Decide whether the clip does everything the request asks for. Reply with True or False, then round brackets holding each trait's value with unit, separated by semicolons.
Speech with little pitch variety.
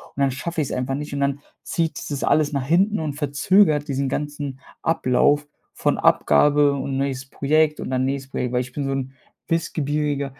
True (2.0 semitones)